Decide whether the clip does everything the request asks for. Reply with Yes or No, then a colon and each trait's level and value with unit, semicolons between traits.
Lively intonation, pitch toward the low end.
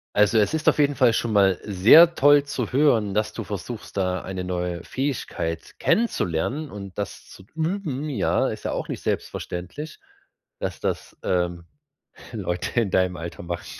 Yes: wide, 7.6 semitones; low, 105 Hz